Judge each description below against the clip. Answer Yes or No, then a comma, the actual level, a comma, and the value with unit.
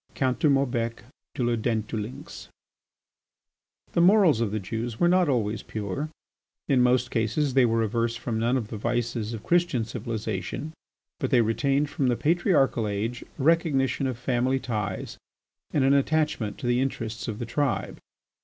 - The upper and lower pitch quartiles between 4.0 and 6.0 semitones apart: No, average, 3.5 semitones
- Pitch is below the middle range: Yes, low, 120 Hz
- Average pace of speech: Yes, average, 165 wpm